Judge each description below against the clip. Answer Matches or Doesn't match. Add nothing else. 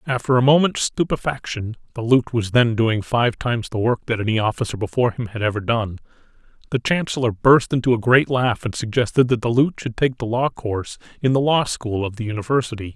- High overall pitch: Doesn't match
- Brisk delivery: Matches